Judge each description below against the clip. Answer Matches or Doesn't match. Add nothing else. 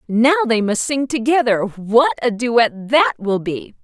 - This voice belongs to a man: Doesn't match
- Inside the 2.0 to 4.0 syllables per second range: Matches